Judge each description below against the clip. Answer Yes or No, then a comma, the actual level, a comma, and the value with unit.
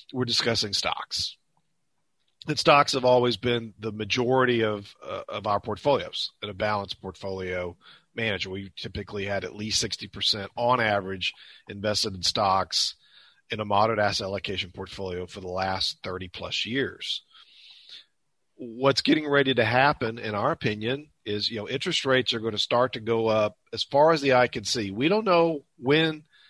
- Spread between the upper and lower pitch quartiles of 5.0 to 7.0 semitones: No, average, 4.1 semitones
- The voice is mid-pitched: No, low, 110 Hz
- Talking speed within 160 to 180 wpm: Yes, average, 170 wpm